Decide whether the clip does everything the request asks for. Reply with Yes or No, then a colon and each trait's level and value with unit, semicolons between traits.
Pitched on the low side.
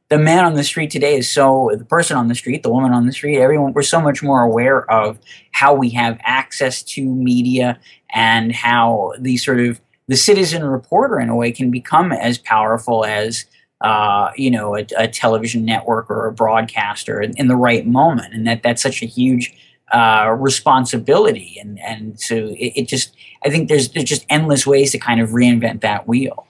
Yes: low, 120 Hz